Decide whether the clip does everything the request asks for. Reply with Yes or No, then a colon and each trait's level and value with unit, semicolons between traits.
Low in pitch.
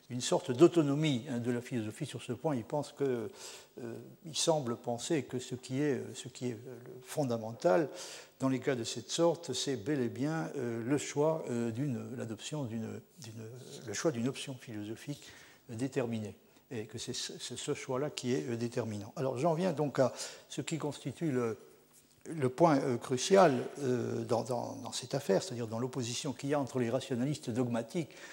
Yes: low, 130 Hz